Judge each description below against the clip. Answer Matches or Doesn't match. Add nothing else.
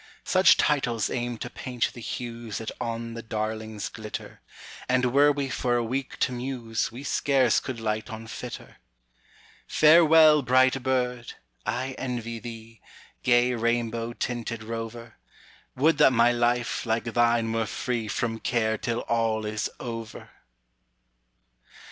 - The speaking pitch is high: Doesn't match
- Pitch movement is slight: Matches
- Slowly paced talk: Matches